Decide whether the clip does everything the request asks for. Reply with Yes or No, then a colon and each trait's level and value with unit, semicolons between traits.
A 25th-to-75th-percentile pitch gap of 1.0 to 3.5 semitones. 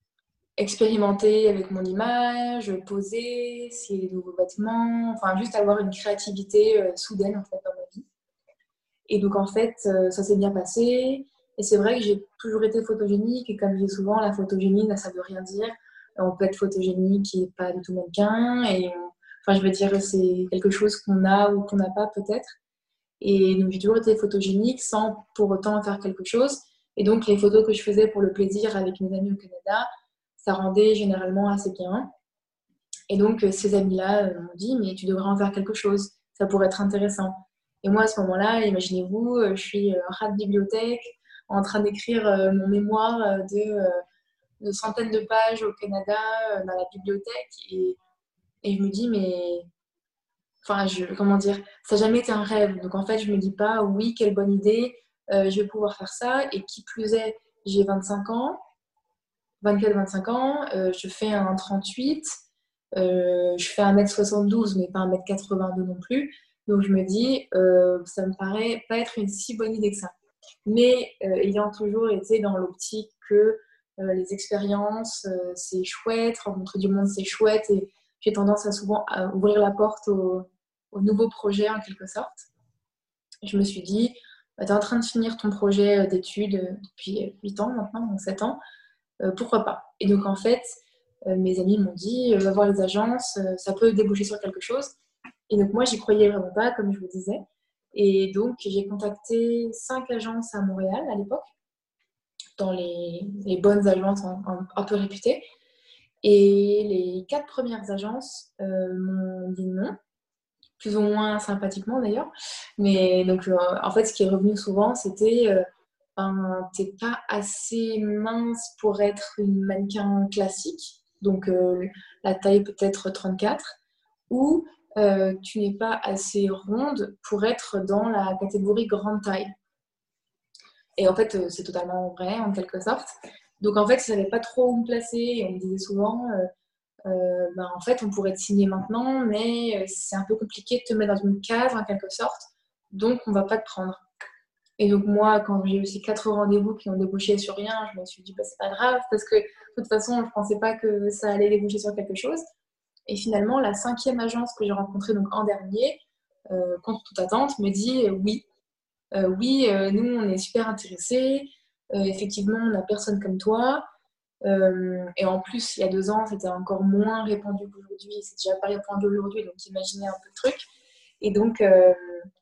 Yes: narrow, 2.4 semitones